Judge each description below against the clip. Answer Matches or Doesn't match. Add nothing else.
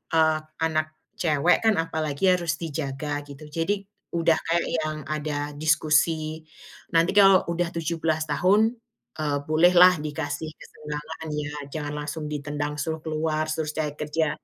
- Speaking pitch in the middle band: Matches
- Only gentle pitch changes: Matches